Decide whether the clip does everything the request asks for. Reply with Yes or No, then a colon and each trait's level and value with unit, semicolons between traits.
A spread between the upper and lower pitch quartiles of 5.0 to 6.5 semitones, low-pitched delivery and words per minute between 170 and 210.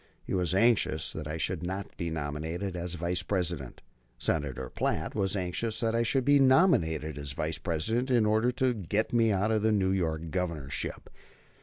Yes: wide, 5.6 semitones; very low, 90 Hz; average, 180 wpm